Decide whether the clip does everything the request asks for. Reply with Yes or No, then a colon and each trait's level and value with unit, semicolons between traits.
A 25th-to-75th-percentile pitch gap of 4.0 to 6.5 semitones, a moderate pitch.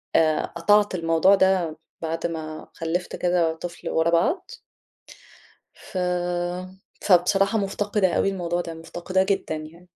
No: average, 2.8 semitones; medium, 175 Hz